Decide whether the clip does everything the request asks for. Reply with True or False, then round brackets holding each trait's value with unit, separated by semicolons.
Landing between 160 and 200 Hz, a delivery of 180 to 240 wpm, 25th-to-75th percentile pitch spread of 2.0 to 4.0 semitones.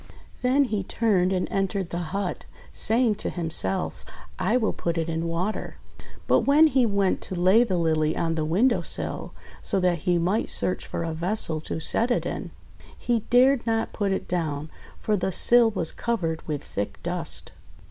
False (185 Hz; 185 wpm; 5.2 semitones)